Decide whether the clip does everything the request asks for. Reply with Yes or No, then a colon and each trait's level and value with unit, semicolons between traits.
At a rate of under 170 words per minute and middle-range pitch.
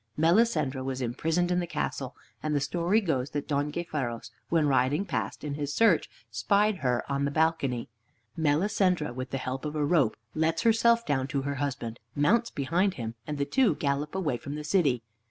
No: average, 190 wpm; medium, 150 Hz